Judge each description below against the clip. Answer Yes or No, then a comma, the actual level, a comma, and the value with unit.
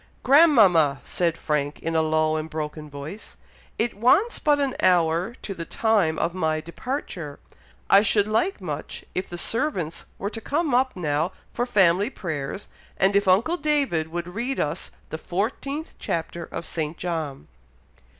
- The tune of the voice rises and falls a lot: Yes, wide, 6.8 semitones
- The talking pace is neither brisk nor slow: Yes, average, 160 wpm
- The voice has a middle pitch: Yes, medium, 180 Hz